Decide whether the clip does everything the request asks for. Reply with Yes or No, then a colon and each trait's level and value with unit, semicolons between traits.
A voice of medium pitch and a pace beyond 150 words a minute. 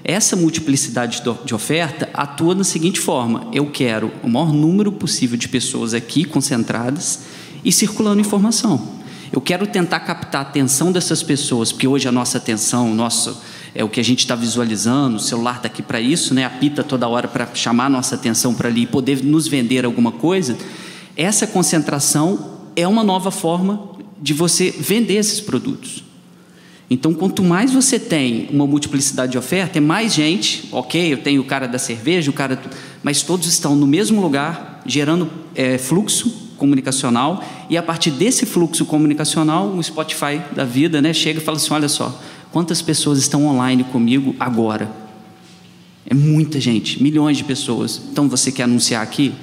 Yes: medium, 145 Hz; average, 170 wpm